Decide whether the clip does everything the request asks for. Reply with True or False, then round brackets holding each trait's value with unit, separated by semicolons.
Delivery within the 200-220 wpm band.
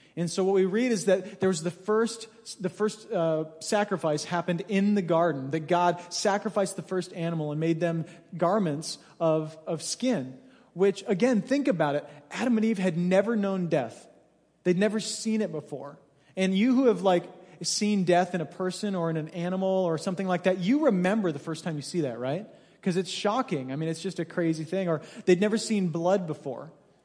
True (205 wpm)